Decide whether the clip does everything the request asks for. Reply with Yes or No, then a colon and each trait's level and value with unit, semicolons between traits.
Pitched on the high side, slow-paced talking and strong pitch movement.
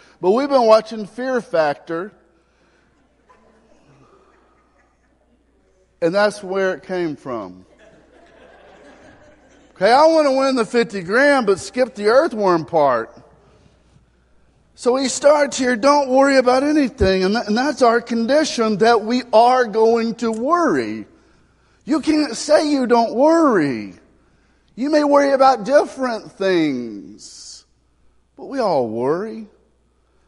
Yes: high, 230 Hz; slow, 115 wpm; wide, 7.2 semitones